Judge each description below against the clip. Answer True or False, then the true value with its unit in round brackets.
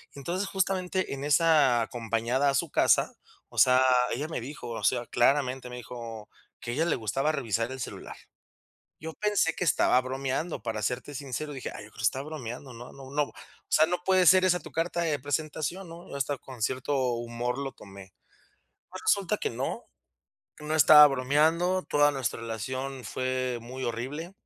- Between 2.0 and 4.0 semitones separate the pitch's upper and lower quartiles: False (4.4 semitones)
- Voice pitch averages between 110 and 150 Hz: True (135 Hz)